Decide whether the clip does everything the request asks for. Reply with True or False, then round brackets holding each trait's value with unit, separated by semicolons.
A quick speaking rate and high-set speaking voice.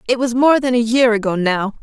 True (265 wpm; 235 Hz)